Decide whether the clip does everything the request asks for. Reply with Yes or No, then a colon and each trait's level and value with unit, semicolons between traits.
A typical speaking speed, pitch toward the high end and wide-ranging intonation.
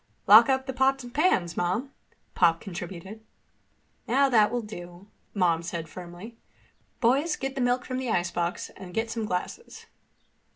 Yes: average, 155 wpm; high, 220 Hz; wide, 6.7 semitones